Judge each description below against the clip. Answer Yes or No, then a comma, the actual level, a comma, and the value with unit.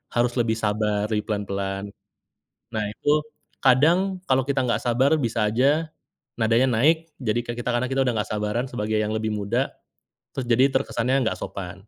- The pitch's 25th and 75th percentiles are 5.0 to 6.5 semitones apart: No, average, 3.8 semitones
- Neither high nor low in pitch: No, low, 120 Hz